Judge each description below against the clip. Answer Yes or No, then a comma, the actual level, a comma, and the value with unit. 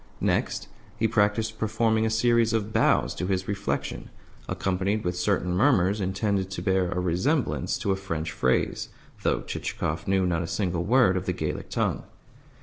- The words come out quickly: No, average, 165 wpm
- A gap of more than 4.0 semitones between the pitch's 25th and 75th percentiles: No, average, 3.4 semitones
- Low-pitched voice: Yes, very low, 95 Hz